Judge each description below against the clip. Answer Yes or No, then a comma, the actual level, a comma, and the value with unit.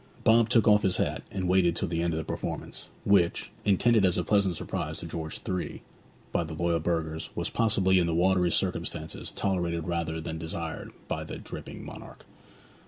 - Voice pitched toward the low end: Yes, very low, 85 Hz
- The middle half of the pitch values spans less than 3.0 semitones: Yes, narrow, 2.6 semitones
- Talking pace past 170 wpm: Yes, average, 185 wpm